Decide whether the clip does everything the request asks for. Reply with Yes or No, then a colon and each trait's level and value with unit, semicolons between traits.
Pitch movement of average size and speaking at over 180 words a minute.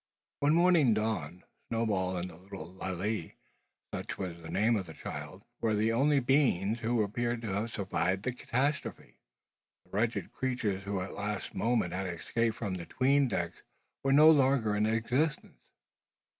No: average, 4.6 semitones; average, 165 wpm